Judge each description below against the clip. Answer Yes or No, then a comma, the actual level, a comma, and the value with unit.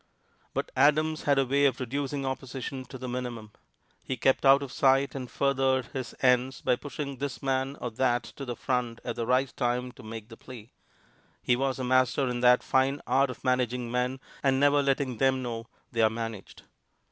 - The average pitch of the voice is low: Yes, low, 130 Hz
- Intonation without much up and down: Yes, narrow, 1.8 semitones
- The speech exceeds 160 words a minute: Yes, average, 195 wpm